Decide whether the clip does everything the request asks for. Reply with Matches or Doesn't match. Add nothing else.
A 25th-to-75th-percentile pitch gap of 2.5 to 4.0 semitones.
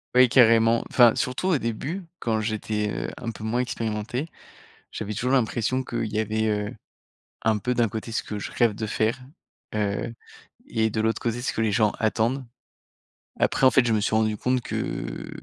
Doesn't match